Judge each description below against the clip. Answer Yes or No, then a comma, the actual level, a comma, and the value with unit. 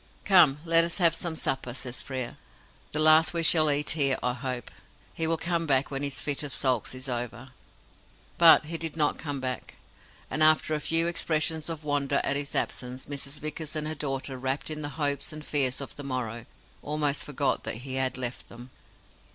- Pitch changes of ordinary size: Yes, average, 3.1 semitones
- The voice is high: No, medium, 145 Hz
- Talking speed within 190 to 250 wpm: Yes, average, 200 wpm